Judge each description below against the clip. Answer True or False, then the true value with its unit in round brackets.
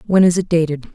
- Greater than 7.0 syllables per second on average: False (6.7 syllables/s)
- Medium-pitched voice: True (170 Hz)